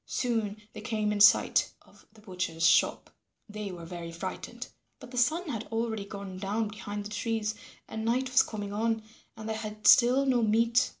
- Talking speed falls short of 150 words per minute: No, average, 185 wpm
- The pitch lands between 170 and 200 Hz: No, high, 215 Hz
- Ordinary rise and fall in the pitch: No, narrow, 2.1 semitones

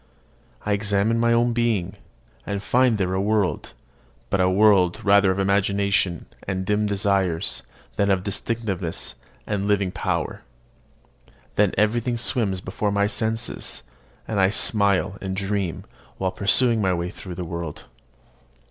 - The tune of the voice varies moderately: No, narrow, 2.1 semitones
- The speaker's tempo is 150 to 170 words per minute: No, average, 140 wpm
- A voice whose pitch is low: Yes, low, 100 Hz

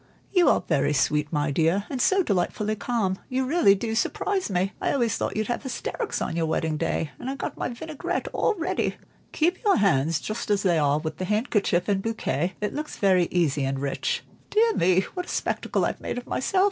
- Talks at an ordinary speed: No, fast, 210 wpm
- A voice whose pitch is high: Yes, high, 205 Hz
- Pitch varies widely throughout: Yes, wide, 8.1 semitones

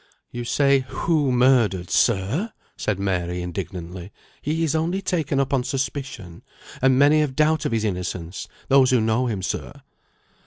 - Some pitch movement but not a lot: No, wide, 6.9 semitones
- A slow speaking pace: No, average, 160 wpm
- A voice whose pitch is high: No, low, 125 Hz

